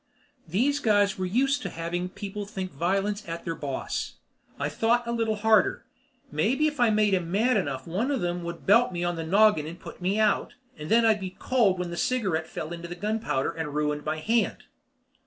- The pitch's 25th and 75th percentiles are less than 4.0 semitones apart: No, average, 4.6 semitones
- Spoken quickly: Yes, fast, 210 wpm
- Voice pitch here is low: No, high, 195 Hz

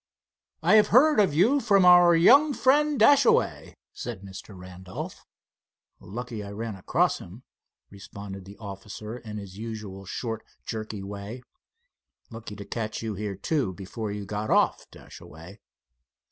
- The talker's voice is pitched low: Yes, low, 110 Hz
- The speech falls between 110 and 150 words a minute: Yes, average, 140 wpm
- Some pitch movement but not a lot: No, wide, 8.9 semitones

